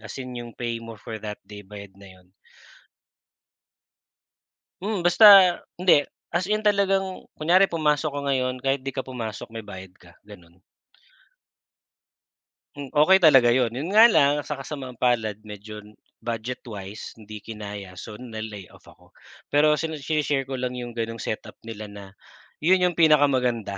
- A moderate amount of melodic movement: No, wide, 6.1 semitones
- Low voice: Yes, low, 125 Hz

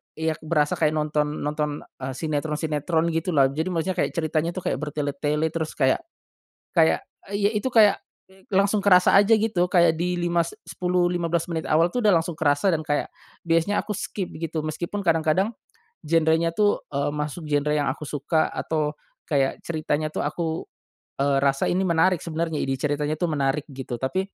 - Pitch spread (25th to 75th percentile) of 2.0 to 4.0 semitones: Yes, average, 2.9 semitones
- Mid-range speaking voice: Yes, medium, 160 Hz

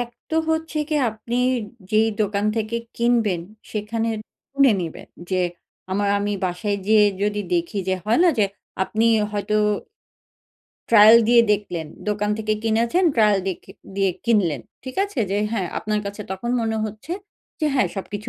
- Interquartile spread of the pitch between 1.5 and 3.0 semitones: Yes, narrow, 2.4 semitones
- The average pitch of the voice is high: Yes, high, 215 Hz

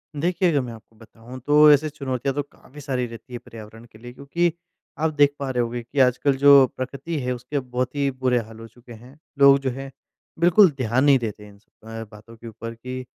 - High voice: No, low, 130 Hz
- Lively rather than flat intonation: No, average, 3.5 semitones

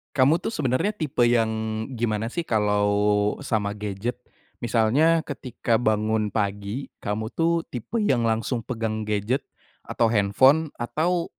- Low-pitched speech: Yes, low, 115 Hz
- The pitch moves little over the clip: No, average, 4.5 semitones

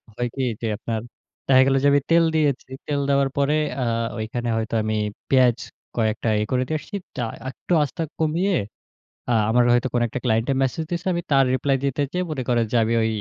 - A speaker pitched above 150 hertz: No, low, 130 Hz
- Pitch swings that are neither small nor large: Yes, average, 3.5 semitones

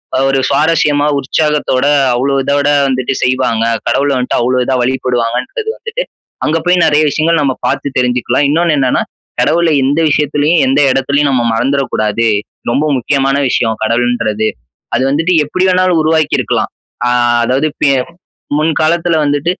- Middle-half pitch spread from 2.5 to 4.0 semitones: Yes, average, 3.5 semitones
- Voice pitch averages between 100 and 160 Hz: Yes, medium, 140 Hz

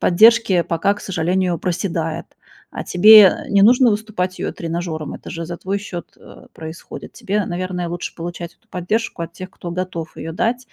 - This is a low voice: No, medium, 180 Hz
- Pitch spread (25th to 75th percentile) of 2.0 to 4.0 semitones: Yes, average, 3.0 semitones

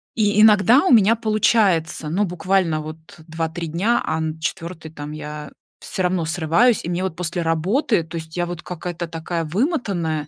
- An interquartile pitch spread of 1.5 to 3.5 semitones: No, average, 3.9 semitones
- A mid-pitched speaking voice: Yes, medium, 175 Hz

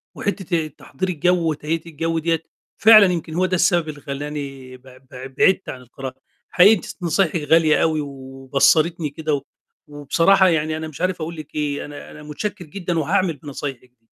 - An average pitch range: Yes, average, 3.4 semitones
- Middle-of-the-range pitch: Yes, medium, 155 Hz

